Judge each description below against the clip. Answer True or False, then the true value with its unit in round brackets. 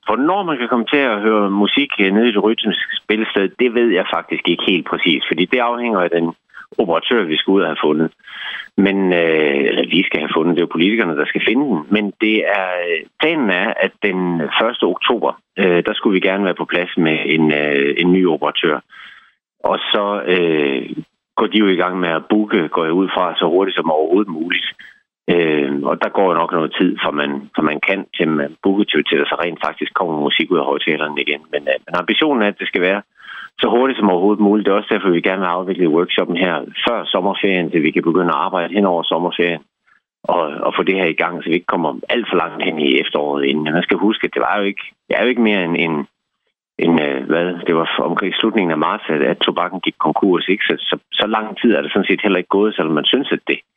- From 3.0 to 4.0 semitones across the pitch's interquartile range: False (4.5 semitones)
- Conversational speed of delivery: False (240 wpm)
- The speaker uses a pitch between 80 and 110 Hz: True (95 Hz)